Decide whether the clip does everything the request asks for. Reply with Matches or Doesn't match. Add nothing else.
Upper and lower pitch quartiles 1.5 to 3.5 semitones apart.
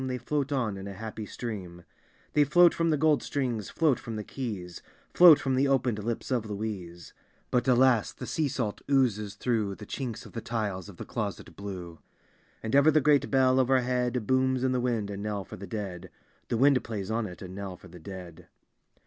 Doesn't match